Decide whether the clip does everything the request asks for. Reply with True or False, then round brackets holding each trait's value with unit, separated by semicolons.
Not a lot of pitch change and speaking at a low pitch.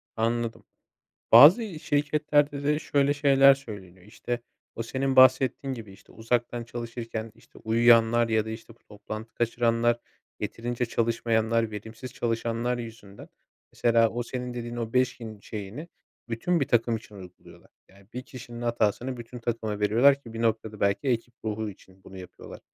True (2.2 semitones; 115 Hz)